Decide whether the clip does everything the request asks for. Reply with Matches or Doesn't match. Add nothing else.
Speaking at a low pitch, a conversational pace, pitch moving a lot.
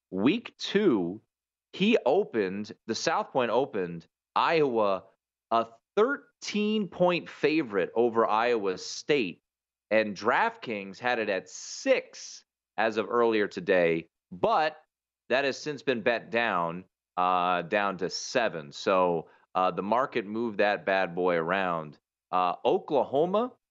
Doesn't match